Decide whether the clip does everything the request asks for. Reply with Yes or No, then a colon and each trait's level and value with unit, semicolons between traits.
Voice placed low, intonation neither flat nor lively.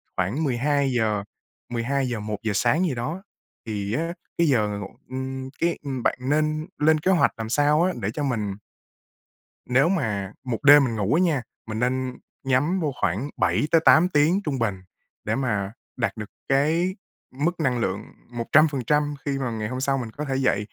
Yes: low, 130 Hz; average, 5.0 semitones